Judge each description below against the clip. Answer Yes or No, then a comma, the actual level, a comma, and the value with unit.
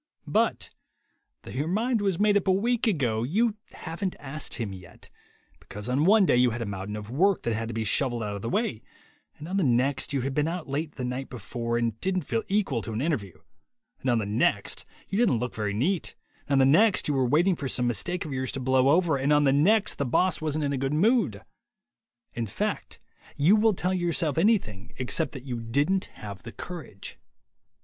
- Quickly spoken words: Yes, fast, 220 wpm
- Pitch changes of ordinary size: No, wide, 7.3 semitones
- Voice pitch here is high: No, medium, 140 Hz